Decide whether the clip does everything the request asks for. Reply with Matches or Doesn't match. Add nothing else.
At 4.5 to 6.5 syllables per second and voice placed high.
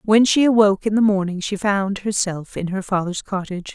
Matches